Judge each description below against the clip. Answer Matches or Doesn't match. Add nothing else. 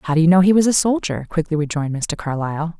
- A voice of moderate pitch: Matches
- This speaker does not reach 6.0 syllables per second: Doesn't match